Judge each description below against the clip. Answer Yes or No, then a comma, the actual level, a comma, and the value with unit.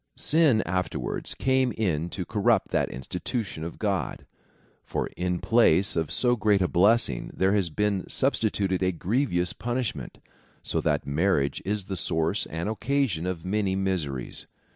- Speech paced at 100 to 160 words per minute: Yes, average, 150 wpm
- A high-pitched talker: No, very low, 95 Hz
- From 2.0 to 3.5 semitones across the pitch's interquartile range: No, average, 4.2 semitones